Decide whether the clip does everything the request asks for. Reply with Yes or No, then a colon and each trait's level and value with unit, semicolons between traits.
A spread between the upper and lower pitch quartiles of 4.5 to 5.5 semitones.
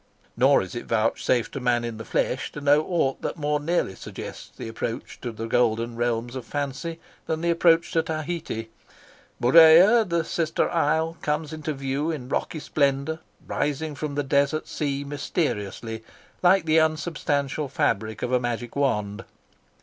Yes: average, 4.8 semitones